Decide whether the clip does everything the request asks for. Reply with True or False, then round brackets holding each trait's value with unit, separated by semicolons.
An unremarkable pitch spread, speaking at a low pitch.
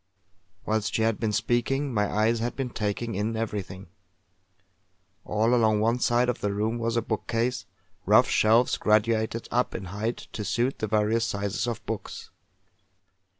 False (2.0 semitones; 115 Hz)